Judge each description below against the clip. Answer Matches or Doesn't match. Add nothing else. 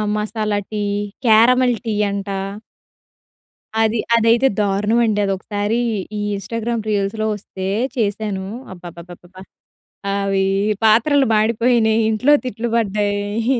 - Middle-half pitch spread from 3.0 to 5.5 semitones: Doesn't match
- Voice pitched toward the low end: Doesn't match